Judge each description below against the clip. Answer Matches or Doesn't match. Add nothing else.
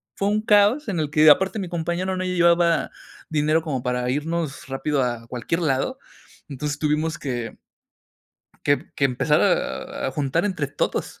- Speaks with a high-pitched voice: Doesn't match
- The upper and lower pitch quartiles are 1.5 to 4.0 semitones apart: Doesn't match